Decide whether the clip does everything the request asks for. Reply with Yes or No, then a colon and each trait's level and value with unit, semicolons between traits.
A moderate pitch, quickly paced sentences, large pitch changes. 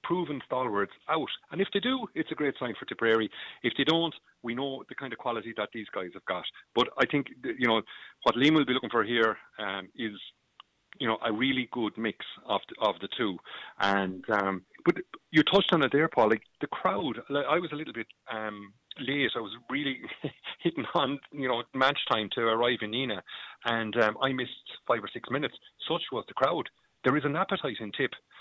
No: low, 130 Hz; fast, 215 wpm; wide, 5.7 semitones